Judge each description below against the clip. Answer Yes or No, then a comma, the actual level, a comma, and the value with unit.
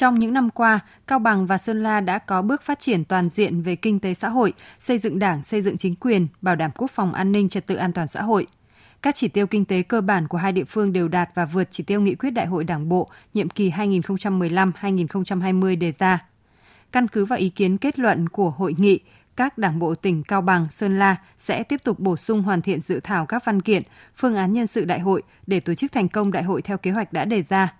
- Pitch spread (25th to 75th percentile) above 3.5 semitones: No, average, 2.7 semitones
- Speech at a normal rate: No, fast, 255 wpm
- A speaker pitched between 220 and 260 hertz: No, high, 195 Hz